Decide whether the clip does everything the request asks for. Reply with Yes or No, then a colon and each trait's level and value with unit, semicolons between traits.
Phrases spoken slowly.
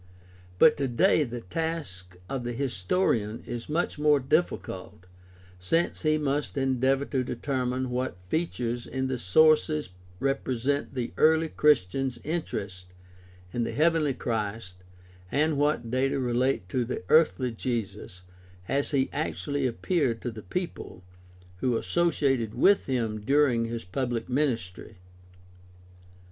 Yes: slow, 125 wpm